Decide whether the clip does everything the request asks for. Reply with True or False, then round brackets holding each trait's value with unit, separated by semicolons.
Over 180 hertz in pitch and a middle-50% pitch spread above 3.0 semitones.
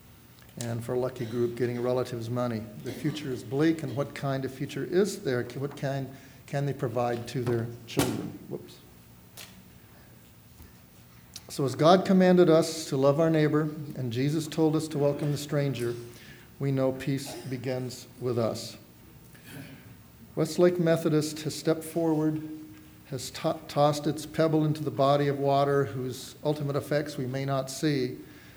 False (135 Hz; 3.8 semitones)